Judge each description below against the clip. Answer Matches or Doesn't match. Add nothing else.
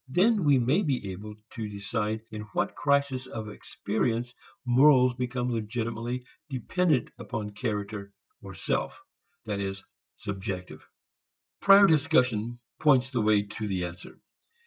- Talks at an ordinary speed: Doesn't match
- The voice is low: Matches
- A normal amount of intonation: Matches